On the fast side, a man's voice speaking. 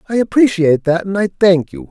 Yes: fast, 220 wpm; male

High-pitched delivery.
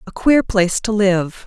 Yes: high, 205 Hz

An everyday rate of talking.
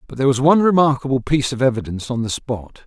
No: fast, 230 wpm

